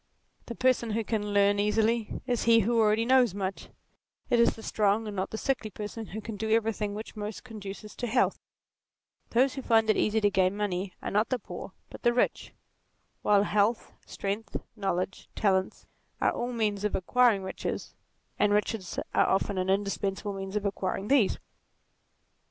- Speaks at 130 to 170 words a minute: No, average, 185 wpm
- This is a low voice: No, high, 210 Hz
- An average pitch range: No, narrow, 2.3 semitones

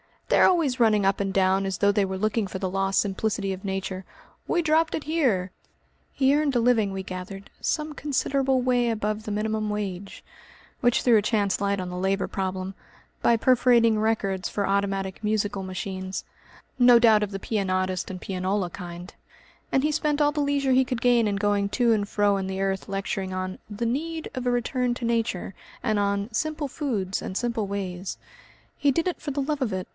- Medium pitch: No, high, 210 Hz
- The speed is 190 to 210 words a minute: Yes, average, 200 wpm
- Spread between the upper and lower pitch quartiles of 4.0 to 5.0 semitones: Yes, average, 4.4 semitones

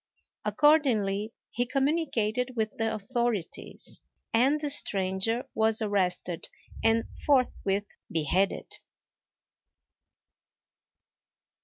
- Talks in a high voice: Yes, high, 225 Hz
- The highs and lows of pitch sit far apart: No, average, 4.2 semitones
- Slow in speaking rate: Yes, slow, 70 wpm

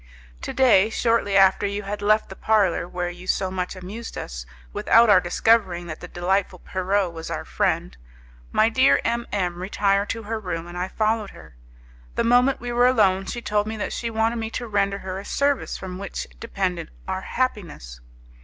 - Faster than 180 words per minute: Yes, average, 190 wpm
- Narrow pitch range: No, average, 3.6 semitones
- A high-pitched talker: Yes, high, 200 Hz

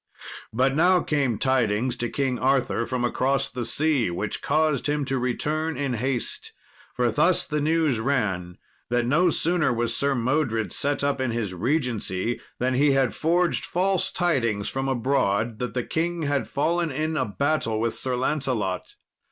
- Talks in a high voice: No, low, 135 Hz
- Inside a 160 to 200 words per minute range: Yes, average, 165 wpm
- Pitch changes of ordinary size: Yes, average, 4.2 semitones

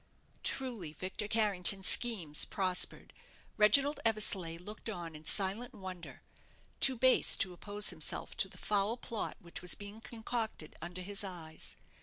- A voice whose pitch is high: Yes, high, 200 Hz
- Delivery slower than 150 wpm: Yes, average, 140 wpm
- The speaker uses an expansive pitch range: No, average, 3.8 semitones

